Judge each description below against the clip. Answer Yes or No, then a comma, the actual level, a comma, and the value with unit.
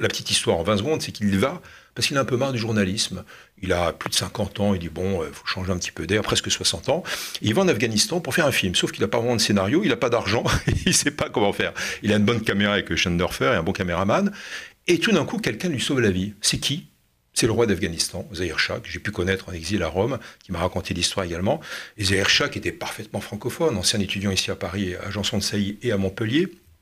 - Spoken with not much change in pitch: No, average, 3.2 semitones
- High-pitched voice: No, low, 100 Hz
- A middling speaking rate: No, fast, 270 wpm